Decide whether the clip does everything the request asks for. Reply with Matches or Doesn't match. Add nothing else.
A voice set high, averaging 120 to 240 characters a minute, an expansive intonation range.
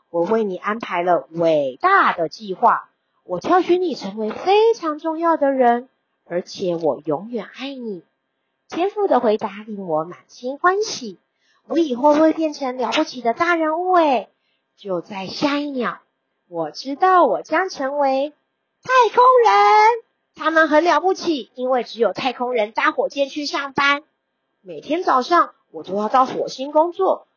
Matches